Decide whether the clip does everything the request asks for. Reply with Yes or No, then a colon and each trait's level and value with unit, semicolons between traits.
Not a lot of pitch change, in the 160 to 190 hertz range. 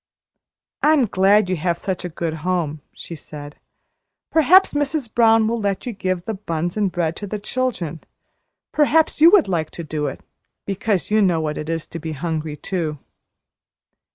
No: wide, 5.5 semitones; medium, 185 Hz